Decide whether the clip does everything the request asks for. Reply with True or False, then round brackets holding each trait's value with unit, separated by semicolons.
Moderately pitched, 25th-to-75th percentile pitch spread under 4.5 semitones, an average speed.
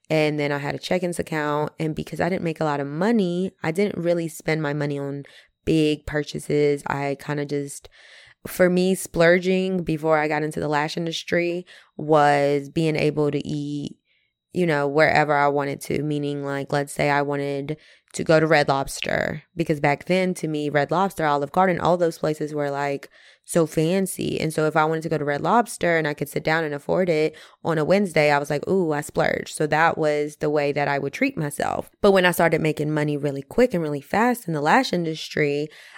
False (155 Hz; 2.9 semitones; 215 wpm)